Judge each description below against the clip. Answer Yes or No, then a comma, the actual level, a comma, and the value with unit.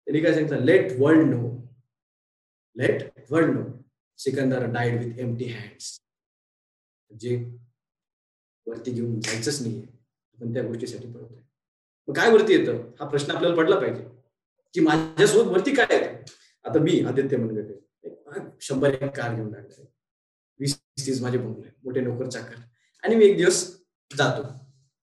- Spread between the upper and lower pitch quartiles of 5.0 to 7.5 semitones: No, average, 3.6 semitones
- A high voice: No, low, 130 Hz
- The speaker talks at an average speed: No, fast, 145 wpm